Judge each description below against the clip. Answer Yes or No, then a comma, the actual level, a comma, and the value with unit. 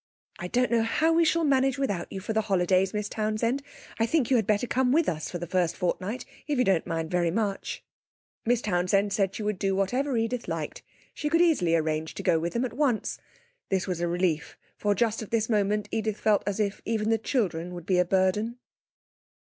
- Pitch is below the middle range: No, high, 210 Hz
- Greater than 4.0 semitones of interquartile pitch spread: Yes, average, 4.6 semitones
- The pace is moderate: No, fast, 215 wpm